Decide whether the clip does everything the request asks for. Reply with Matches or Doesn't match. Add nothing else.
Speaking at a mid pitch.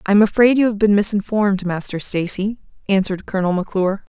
Doesn't match